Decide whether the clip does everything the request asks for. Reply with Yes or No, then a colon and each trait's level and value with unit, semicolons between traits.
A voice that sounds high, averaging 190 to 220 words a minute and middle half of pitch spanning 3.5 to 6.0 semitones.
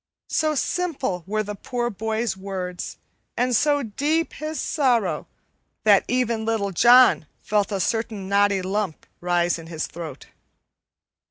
No: high, 215 Hz; slow, 135 wpm; average, 4.7 semitones